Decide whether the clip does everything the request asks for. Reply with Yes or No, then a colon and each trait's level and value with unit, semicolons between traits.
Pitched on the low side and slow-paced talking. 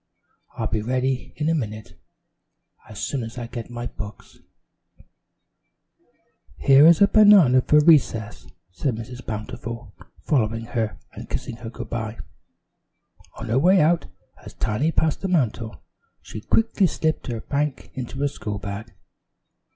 No: low, 125 Hz; average, 145 wpm